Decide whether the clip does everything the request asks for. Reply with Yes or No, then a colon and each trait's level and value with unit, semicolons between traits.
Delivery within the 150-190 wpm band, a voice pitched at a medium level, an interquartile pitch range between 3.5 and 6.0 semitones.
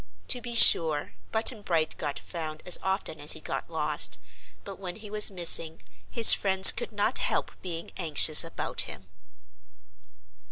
Yes: average, 155 wpm; medium, 180 Hz; average, 4.6 semitones